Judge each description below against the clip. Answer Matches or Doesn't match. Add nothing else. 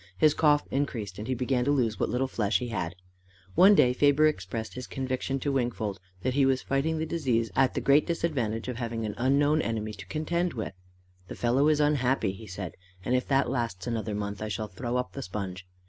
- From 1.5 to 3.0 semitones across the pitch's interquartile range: Doesn't match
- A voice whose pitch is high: Doesn't match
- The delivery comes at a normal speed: Doesn't match